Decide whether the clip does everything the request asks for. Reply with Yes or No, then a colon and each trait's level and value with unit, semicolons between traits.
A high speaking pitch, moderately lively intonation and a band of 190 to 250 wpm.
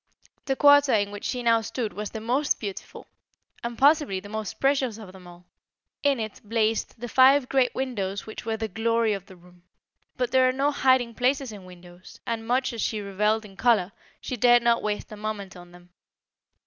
Yes: high, 225 Hz; average, 4.0 semitones; average, 200 wpm